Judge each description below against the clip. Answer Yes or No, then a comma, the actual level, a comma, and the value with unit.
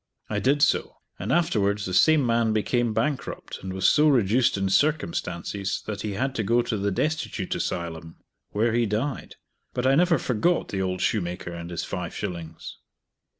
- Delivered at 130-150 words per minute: No, average, 175 wpm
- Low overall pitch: Yes, low, 110 Hz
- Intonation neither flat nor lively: No, wide, 5.7 semitones